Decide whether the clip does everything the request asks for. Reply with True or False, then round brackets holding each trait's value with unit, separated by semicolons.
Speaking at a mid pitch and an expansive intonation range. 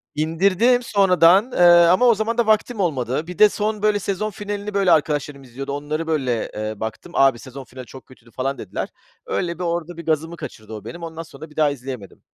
True (165 Hz; 6.5 semitones)